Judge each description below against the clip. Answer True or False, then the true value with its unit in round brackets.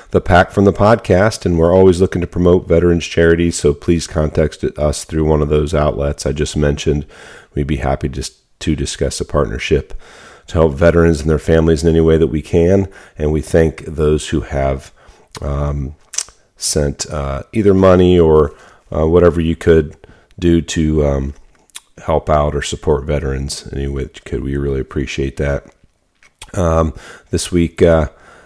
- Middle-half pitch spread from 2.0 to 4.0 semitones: True (2.8 semitones)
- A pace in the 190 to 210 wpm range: False (170 wpm)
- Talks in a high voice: False (80 Hz)